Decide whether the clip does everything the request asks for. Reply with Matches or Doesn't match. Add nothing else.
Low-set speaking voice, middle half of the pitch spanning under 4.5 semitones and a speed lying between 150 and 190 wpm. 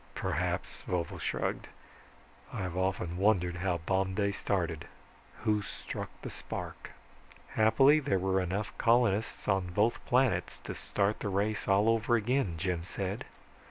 Doesn't match